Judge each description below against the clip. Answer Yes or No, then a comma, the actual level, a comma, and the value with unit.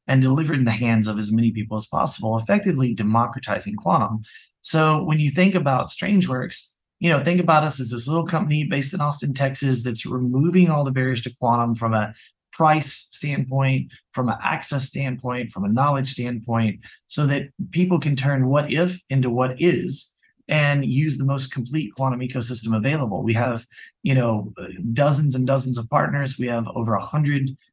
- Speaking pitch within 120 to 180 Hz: Yes, low, 135 Hz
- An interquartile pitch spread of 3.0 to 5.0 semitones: Yes, average, 4.1 semitones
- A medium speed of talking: Yes, average, 180 wpm